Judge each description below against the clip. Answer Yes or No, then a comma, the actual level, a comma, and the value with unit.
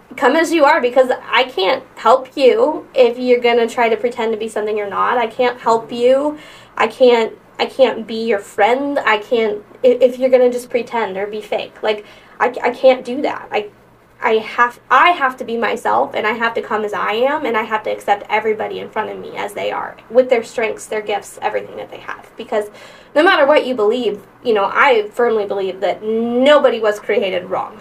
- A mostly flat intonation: No, average, 3.4 semitones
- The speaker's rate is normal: No, fast, 225 wpm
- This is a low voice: No, high, 240 Hz